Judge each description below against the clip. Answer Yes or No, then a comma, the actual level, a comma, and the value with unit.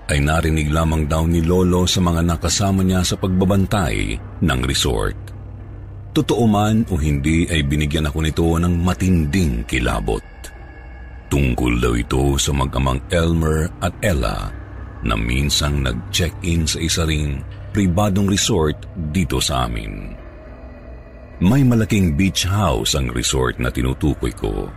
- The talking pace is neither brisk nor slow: Yes, average, 130 wpm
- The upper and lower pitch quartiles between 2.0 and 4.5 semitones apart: No, average, 5.2 semitones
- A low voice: Yes, very low, 85 Hz